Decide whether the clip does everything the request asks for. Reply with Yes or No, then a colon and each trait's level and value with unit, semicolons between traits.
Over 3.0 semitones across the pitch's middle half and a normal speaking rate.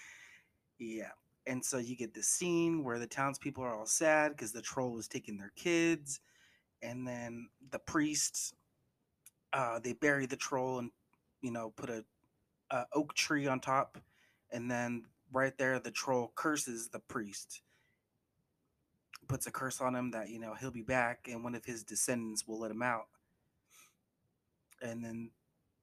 No: average, 2.7 semitones; average, 165 wpm